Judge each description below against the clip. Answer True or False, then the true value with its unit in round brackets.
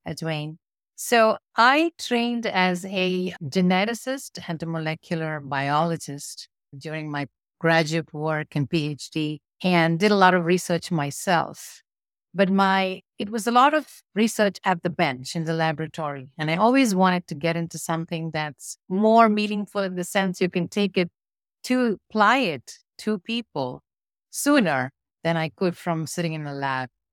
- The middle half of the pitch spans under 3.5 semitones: False (4.7 semitones)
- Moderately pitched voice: True (175 Hz)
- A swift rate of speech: False (155 wpm)